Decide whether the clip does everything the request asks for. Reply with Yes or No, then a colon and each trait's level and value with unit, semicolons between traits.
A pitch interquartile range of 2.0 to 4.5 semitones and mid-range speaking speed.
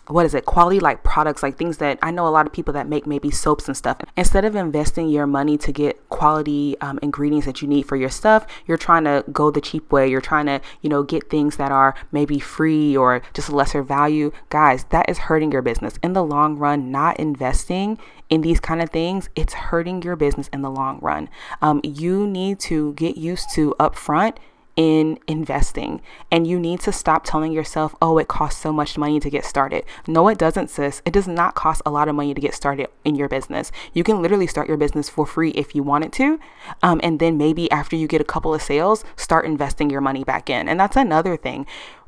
No: narrow, 2.4 semitones; fast, 230 wpm